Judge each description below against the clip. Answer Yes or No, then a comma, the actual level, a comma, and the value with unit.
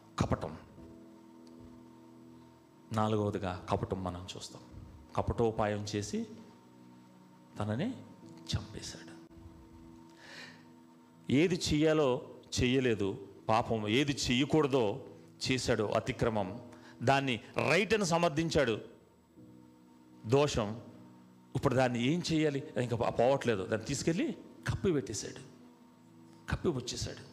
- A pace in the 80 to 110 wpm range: No, slow, 70 wpm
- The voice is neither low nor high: No, low, 105 Hz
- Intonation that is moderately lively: No, wide, 7.5 semitones